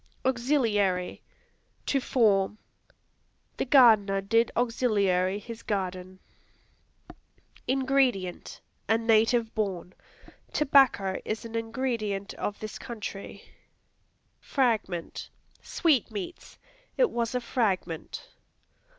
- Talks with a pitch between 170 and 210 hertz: No, high, 225 Hz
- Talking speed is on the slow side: Yes, slow, 80 wpm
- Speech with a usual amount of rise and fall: Yes, average, 4.1 semitones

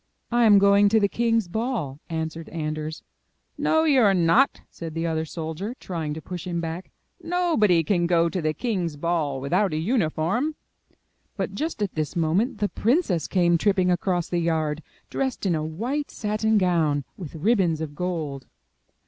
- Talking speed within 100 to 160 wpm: No, average, 170 wpm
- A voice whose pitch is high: No, medium, 175 Hz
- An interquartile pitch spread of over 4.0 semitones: Yes, average, 5.1 semitones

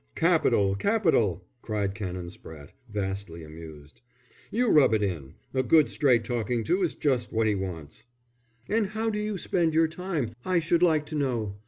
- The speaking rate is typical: Yes, average, 170 wpm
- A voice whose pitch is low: Yes, low, 115 Hz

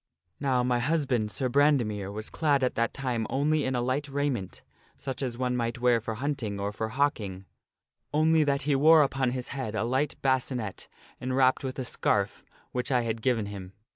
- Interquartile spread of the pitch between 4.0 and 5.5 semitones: No, average, 3.6 semitones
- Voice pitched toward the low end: Yes, low, 125 Hz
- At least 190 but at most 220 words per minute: Yes, average, 195 wpm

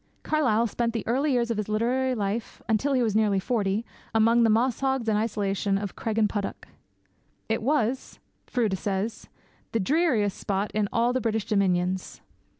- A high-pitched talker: Yes, high, 220 Hz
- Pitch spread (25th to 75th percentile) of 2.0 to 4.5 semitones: Yes, average, 2.9 semitones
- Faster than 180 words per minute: No, average, 155 wpm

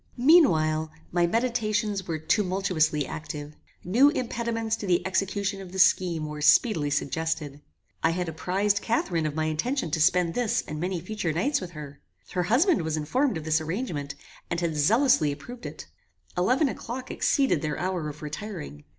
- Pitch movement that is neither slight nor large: No, wide, 6.0 semitones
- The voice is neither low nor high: Yes, medium, 180 Hz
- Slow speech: No, average, 165 wpm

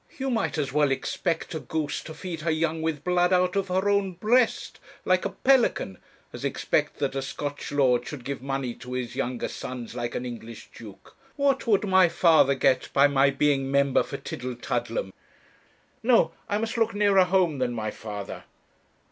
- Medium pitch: Yes, medium, 150 Hz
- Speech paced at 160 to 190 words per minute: Yes, average, 180 wpm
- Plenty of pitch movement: Yes, wide, 6.5 semitones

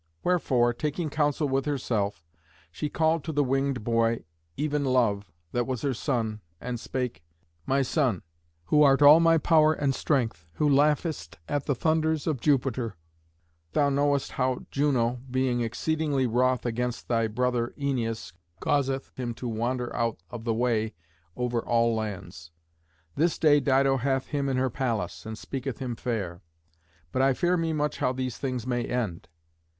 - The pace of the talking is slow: No, average, 160 wpm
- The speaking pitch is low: Yes, low, 130 Hz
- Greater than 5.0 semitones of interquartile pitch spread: No, average, 3.6 semitones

